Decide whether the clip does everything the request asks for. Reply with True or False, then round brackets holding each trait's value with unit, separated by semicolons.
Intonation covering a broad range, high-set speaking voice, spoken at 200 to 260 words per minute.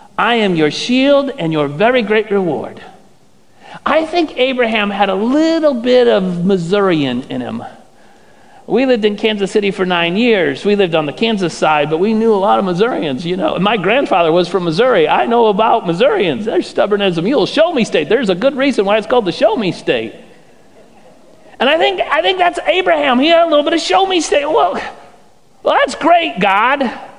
True (6.5 semitones; 225 Hz; 205 wpm)